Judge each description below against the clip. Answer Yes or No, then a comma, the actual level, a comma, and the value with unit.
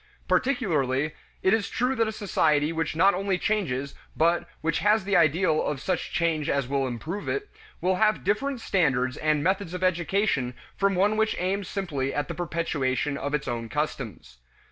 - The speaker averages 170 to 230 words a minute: Yes, average, 175 wpm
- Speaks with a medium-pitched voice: Yes, medium, 170 Hz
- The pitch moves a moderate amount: No, wide, 5.7 semitones